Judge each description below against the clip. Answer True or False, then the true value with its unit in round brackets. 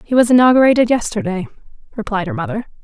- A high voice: True (225 Hz)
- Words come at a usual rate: True (150 wpm)